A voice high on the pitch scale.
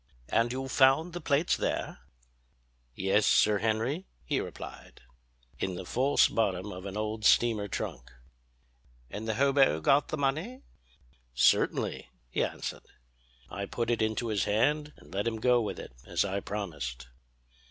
No: low, 110 Hz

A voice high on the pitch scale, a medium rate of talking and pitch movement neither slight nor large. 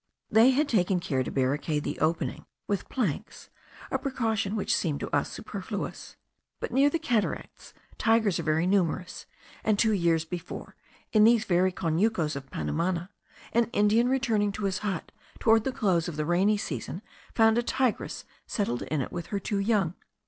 Yes: high, 200 Hz; average, 170 wpm; average, 5.0 semitones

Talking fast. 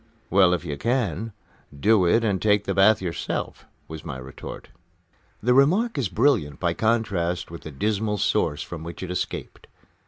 No: average, 165 wpm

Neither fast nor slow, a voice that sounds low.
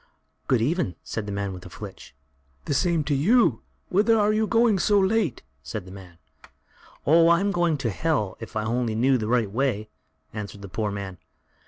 Yes: average, 190 wpm; low, 125 Hz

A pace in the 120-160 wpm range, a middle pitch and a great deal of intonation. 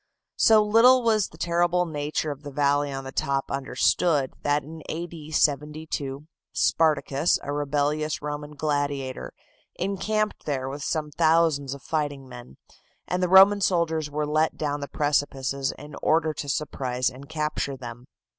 No: average, 155 wpm; medium, 150 Hz; narrow, 2.6 semitones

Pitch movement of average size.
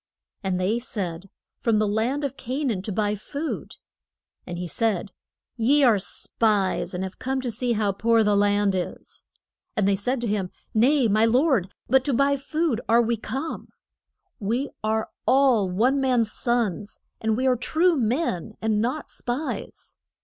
Yes: average, 4.3 semitones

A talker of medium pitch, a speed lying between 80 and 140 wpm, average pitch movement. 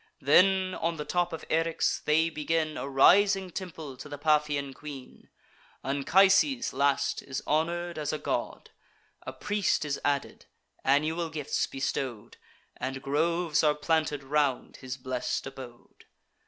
Yes: medium, 150 Hz; slow, 135 wpm; average, 3.3 semitones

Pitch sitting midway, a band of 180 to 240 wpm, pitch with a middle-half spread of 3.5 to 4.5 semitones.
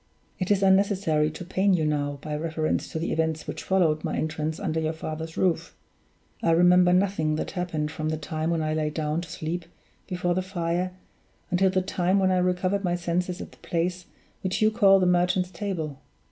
No: medium, 175 Hz; average, 200 wpm; average, 2.8 semitones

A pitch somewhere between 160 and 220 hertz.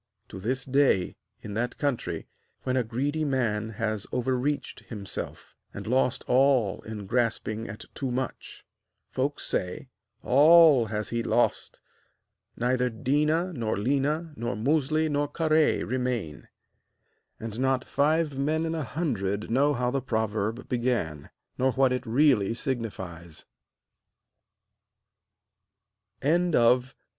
No: low, 125 Hz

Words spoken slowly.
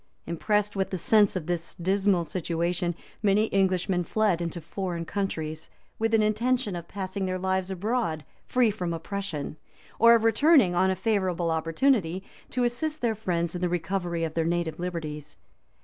No: average, 165 wpm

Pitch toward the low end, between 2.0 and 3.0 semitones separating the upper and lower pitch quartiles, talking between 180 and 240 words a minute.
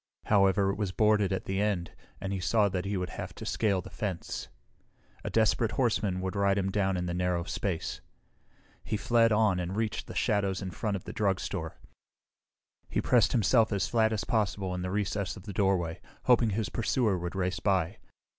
Yes: low, 100 Hz; narrow, 2.6 semitones; average, 195 wpm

